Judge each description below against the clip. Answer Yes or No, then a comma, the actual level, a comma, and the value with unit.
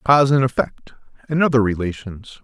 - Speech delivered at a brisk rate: No, average, 175 wpm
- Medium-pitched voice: No, low, 120 Hz